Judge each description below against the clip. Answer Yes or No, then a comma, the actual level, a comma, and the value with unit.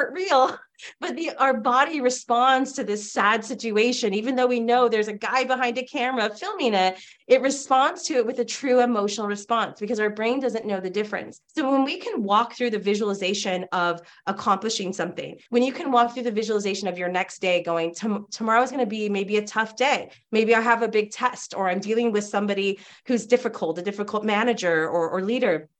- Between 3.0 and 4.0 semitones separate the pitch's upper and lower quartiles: Yes, average, 3.7 semitones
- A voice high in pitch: Yes, high, 220 Hz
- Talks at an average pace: No, fast, 210 wpm